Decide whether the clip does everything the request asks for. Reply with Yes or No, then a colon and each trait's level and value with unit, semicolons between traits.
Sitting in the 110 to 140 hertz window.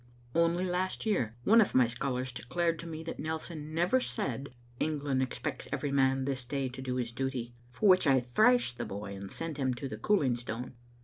Yes: low, 135 Hz